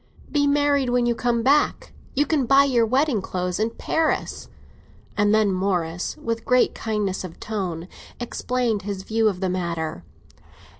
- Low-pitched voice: No, high, 220 Hz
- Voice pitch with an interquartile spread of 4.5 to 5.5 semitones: Yes, average, 5.1 semitones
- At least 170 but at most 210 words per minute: No, average, 155 wpm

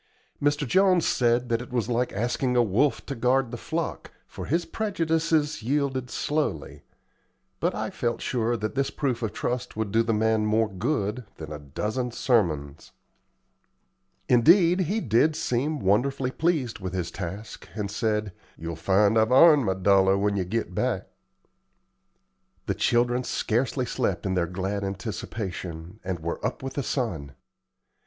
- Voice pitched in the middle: No, low, 115 Hz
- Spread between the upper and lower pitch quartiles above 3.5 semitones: Yes, wide, 5.4 semitones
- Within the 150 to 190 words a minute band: Yes, average, 155 wpm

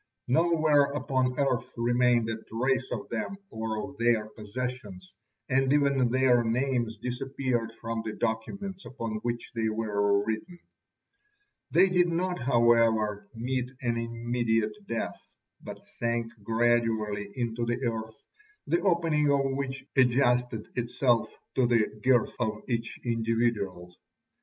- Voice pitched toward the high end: No, low, 120 Hz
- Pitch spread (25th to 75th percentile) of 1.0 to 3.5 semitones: Yes, average, 2.9 semitones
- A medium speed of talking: No, slow, 125 wpm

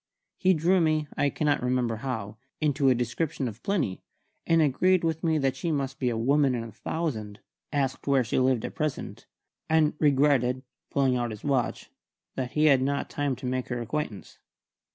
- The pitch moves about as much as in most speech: Yes, average, 3.6 semitones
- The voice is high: No, low, 135 Hz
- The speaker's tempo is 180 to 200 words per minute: Yes, average, 185 wpm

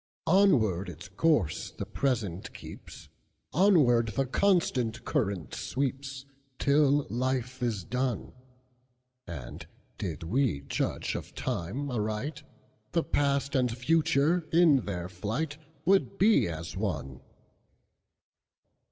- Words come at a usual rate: No, slow, 90 wpm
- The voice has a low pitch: Yes, low, 130 Hz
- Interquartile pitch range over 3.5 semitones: Yes, average, 5.2 semitones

